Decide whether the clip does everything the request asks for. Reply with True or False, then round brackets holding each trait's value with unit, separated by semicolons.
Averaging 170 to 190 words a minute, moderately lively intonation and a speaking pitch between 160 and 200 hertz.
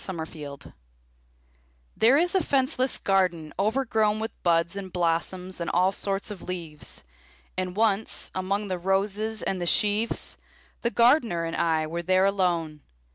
False (145 wpm; 4.0 semitones; 190 Hz)